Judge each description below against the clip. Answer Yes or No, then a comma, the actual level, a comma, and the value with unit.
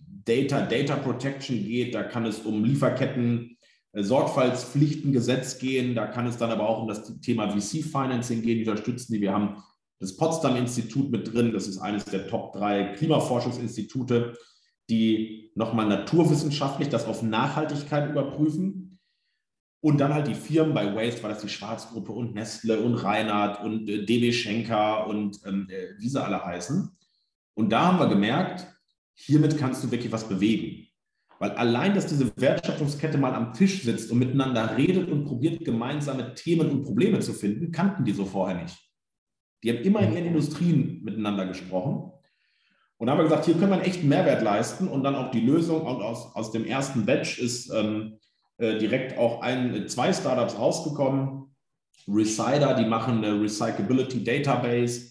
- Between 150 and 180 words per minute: Yes, average, 160 wpm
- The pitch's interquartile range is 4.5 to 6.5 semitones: Yes, average, 4.9 semitones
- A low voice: Yes, low, 120 Hz